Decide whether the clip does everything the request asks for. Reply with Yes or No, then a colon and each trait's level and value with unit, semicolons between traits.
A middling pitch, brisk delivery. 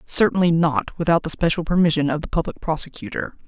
No: medium, 160 Hz; average, 175 wpm